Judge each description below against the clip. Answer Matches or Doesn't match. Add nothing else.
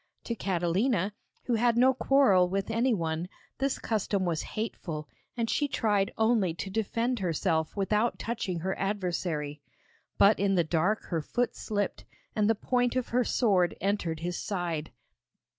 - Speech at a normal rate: Matches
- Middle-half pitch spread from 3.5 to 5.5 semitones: Matches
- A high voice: Matches